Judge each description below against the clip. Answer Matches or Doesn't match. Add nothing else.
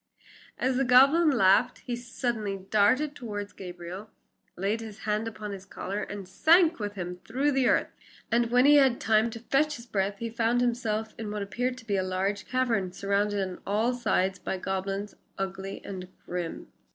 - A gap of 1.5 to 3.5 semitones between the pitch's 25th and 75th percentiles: Doesn't match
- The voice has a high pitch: Matches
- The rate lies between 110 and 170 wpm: Doesn't match